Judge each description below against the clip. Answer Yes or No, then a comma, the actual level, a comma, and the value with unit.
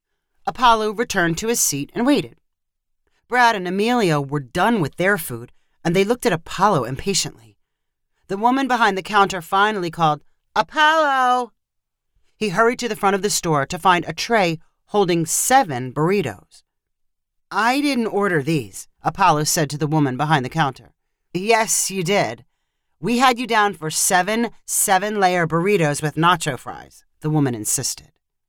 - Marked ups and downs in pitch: Yes, wide, 6.4 semitones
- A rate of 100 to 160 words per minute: Yes, average, 155 wpm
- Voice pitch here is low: No, medium, 185 Hz